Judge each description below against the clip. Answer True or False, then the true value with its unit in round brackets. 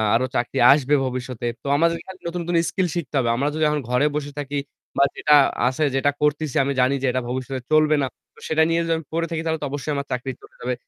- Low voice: False (145 Hz)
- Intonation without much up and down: False (3.4 semitones)